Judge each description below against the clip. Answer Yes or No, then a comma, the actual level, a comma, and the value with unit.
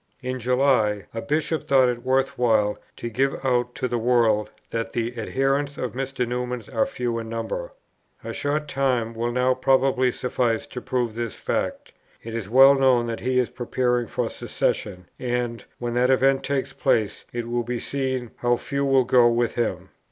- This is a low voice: Yes, low, 125 Hz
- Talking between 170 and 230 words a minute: Yes, average, 180 wpm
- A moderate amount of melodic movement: No, narrow, 2.1 semitones